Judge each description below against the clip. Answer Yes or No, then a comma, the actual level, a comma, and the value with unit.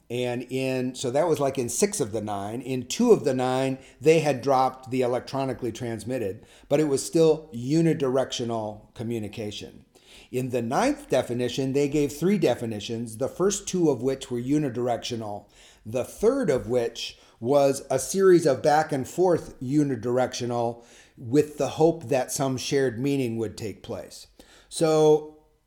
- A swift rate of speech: No, average, 155 wpm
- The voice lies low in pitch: Yes, low, 130 Hz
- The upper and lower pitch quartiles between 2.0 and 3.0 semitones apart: No, average, 3.8 semitones